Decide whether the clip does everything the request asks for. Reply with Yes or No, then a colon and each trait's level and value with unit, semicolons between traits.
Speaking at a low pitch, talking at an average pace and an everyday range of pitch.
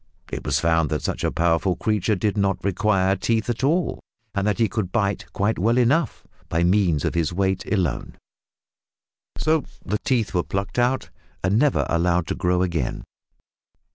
Yes: low, 100 Hz; average, 170 wpm; average, 4.3 semitones